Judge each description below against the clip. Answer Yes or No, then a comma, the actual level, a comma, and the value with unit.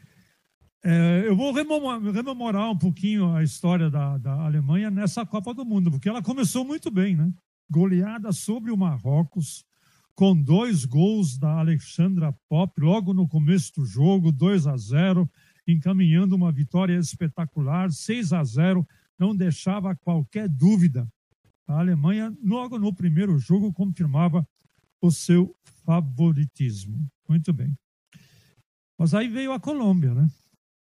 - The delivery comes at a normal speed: Yes, average, 135 wpm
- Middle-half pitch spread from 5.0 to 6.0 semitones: No, average, 4.0 semitones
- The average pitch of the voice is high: No, medium, 175 Hz